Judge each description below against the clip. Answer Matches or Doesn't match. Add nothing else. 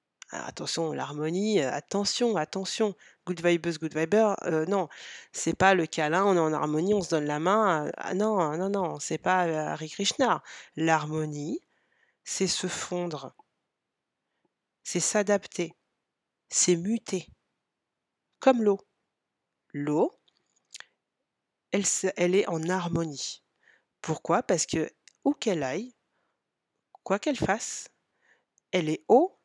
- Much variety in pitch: Doesn't match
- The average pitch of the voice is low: Doesn't match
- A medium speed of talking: Doesn't match